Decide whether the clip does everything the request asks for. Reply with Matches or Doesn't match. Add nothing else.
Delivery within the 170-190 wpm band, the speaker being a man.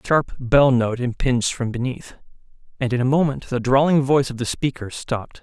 Doesn't match